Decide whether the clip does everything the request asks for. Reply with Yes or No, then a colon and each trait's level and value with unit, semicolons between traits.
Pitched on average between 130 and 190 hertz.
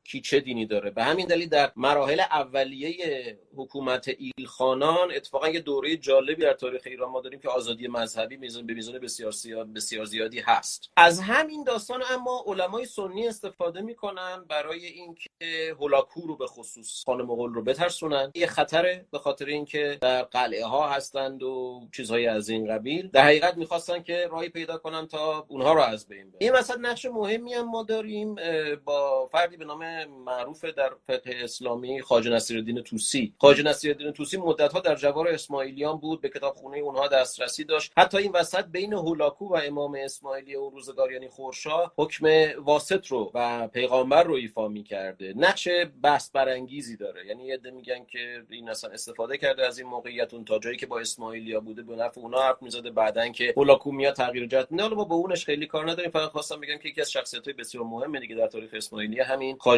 Yes: medium, 140 Hz